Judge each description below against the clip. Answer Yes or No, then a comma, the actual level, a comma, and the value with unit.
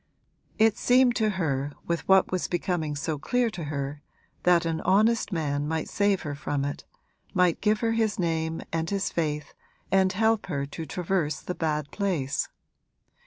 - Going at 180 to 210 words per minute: No, average, 165 wpm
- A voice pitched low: No, medium, 170 Hz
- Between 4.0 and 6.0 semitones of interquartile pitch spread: Yes, average, 5.0 semitones